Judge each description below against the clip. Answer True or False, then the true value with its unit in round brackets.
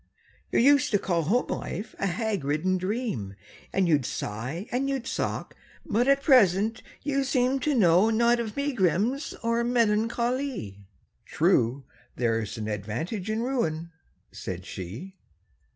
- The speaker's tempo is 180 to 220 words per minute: False (140 wpm)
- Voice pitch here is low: False (210 Hz)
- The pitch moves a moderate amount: False (8.0 semitones)